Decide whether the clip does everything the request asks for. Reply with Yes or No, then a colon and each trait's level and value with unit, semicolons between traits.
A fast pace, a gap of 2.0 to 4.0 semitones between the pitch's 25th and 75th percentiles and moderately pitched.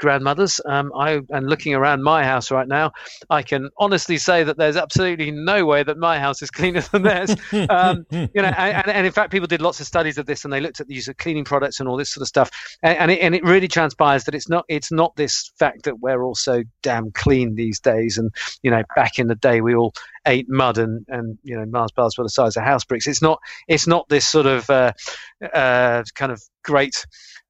No: fast, 245 wpm; average, 4.5 semitones; medium, 145 Hz